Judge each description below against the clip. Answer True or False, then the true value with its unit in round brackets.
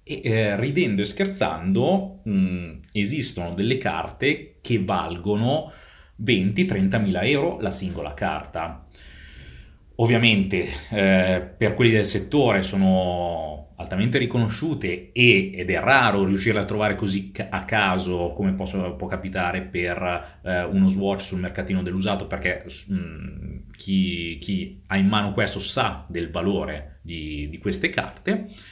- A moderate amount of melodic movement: True (3.0 semitones)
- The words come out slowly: False (130 wpm)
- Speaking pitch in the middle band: False (95 Hz)